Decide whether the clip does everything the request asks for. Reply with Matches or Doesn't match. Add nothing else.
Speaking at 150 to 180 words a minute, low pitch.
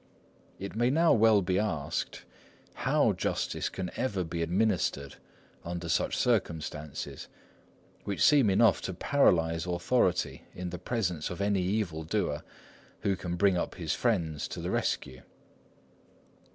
Doesn't match